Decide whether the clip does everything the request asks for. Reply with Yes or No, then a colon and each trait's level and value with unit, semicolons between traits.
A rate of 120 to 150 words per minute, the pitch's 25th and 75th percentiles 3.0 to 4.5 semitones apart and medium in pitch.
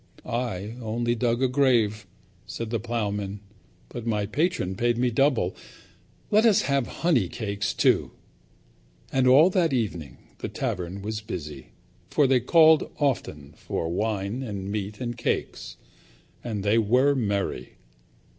No: slow, 135 wpm; average, 4.1 semitones; low, 115 Hz